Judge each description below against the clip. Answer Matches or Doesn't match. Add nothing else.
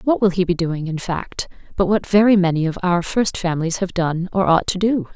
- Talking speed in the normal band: Doesn't match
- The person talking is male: Doesn't match